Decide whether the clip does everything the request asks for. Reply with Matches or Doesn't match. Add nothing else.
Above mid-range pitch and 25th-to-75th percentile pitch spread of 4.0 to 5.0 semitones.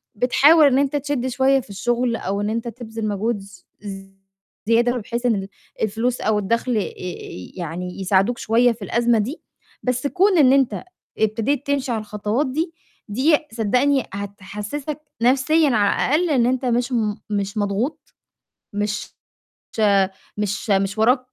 Matches